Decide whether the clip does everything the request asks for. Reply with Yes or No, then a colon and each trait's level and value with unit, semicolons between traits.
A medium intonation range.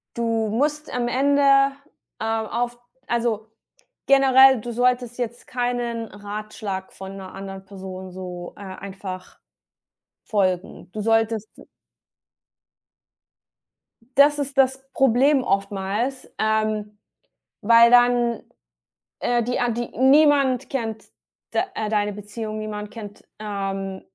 Yes: average, 3.2 semitones